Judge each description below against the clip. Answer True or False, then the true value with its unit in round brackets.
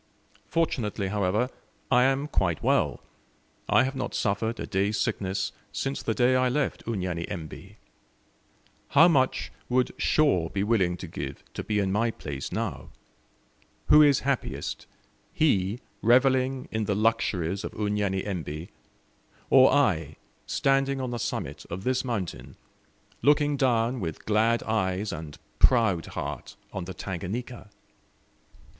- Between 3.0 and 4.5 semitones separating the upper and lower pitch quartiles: False (5.5 semitones)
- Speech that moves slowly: True (130 wpm)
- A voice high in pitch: False (110 Hz)